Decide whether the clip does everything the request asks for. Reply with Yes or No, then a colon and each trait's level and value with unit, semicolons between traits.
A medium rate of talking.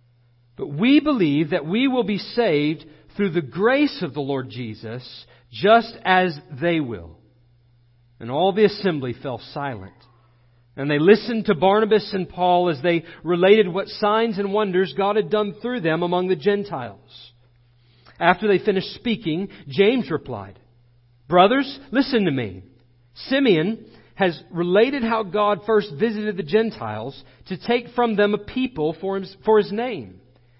Yes: average, 145 wpm